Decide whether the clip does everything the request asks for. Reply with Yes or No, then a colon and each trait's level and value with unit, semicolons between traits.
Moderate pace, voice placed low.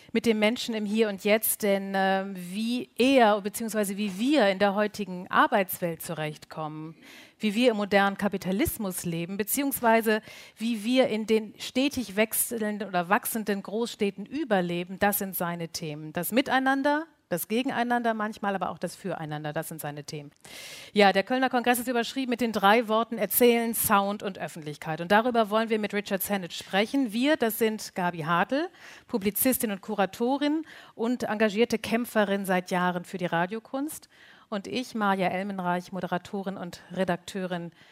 No: average, 155 wpm; high, 210 Hz